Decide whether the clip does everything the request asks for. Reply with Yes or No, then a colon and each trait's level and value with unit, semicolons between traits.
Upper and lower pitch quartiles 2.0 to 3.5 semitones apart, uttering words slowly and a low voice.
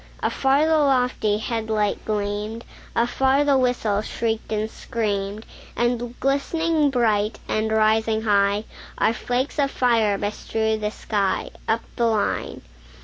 No: average, 2.9 semitones; slow, 130 wpm; high, 225 Hz